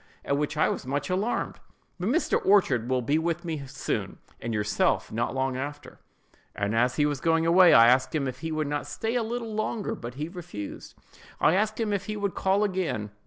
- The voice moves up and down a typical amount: No, wide, 6.9 semitones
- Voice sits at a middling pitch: Yes, medium, 155 Hz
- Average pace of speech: No, fast, 210 wpm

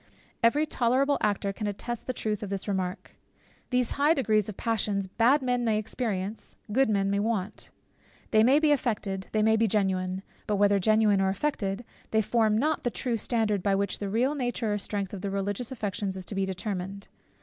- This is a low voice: No, high, 215 Hz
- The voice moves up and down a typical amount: Yes, average, 3.3 semitones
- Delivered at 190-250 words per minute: Yes, average, 200 wpm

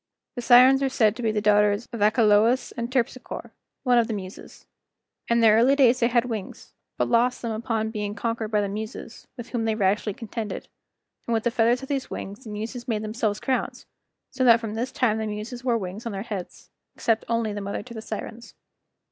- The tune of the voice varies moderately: No, narrow, 2.3 semitones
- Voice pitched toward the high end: Yes, high, 225 Hz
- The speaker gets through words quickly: Yes, fast, 215 wpm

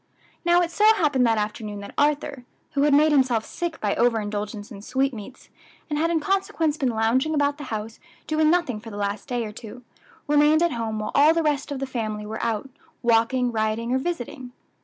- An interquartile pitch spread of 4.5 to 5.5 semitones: Yes, average, 5.2 semitones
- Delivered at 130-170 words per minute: No, fast, 205 wpm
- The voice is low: No, very high, 255 Hz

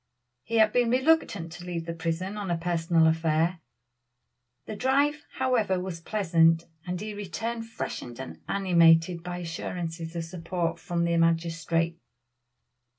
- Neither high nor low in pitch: Yes, medium, 170 Hz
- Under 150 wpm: Yes, average, 140 wpm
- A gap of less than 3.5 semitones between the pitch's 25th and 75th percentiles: No, average, 3.8 semitones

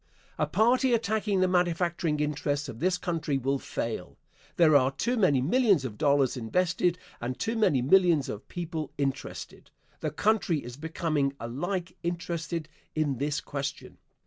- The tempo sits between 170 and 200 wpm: No, average, 145 wpm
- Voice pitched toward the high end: No, medium, 160 Hz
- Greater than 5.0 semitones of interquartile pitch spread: No, average, 4.5 semitones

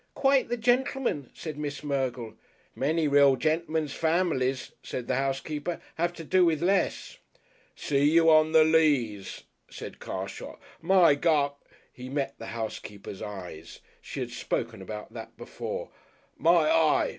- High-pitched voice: No, medium, 150 Hz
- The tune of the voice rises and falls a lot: No, average, 3.9 semitones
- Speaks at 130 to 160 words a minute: Yes, average, 145 wpm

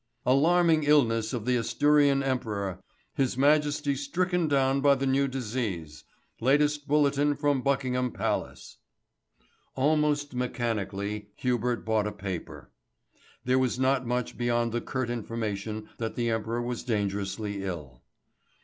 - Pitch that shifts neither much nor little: Yes, average, 4.3 semitones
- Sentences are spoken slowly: Yes, slow, 125 wpm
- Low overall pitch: Yes, low, 125 Hz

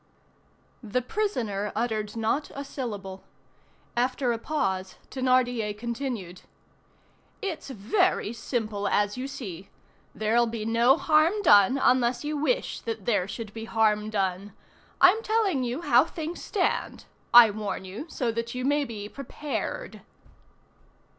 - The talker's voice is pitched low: No, high, 235 Hz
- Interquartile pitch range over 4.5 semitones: Yes, average, 5.0 semitones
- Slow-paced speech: Yes, slow, 130 wpm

